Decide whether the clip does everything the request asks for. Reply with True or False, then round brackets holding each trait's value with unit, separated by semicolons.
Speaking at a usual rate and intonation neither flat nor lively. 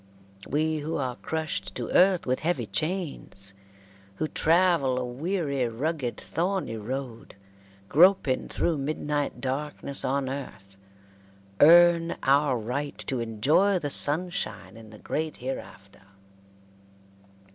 False (115 wpm; 4.5 semitones)